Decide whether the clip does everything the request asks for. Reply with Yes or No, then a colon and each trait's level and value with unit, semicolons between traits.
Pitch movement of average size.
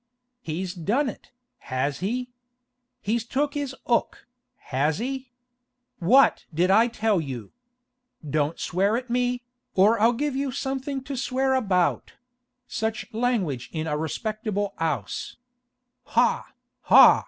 No: wide, 6.6 semitones